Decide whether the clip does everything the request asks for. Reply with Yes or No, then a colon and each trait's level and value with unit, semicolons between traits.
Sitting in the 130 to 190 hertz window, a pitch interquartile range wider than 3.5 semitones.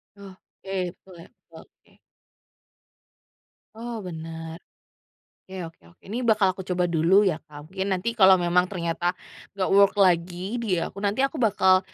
No: medium, 185 Hz; average, 2.7 semitones